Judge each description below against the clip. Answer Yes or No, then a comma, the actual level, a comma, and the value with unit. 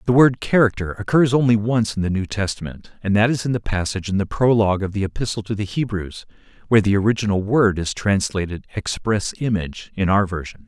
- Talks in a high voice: No, low, 105 Hz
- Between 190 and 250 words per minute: Yes, average, 200 wpm